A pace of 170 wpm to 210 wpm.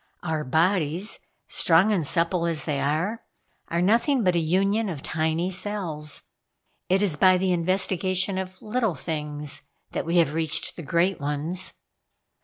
No: average, 150 wpm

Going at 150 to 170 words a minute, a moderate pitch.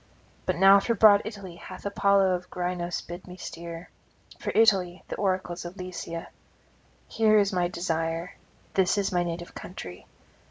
Yes: average, 155 wpm; medium, 180 Hz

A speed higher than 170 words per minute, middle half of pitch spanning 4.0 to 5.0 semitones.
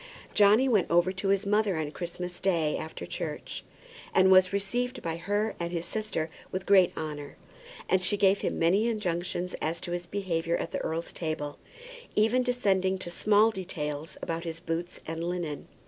No: average, 180 wpm; average, 3.4 semitones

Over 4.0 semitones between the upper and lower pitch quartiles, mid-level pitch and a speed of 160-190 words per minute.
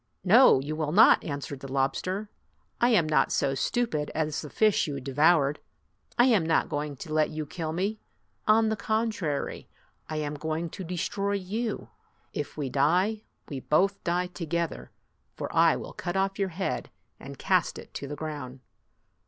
Yes: average, 5.0 semitones; medium, 160 Hz; average, 175 wpm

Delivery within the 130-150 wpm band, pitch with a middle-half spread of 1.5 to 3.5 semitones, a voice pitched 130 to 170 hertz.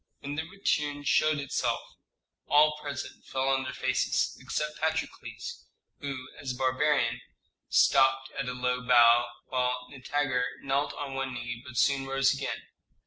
Yes: average, 145 wpm; narrow, 2.5 semitones; low, 135 Hz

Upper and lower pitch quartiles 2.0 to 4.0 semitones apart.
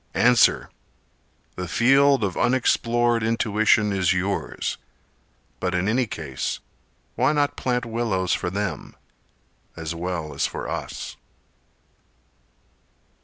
No: average, 4.7 semitones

